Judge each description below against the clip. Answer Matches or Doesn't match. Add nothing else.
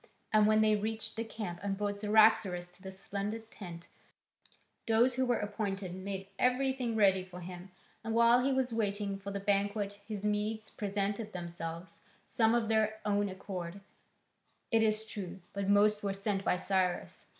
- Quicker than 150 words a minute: Matches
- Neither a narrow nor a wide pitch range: Doesn't match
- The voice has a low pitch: Doesn't match